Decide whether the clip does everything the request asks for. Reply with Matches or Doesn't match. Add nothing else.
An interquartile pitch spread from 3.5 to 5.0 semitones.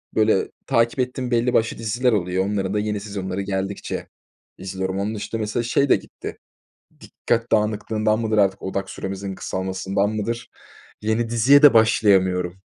Doesn't match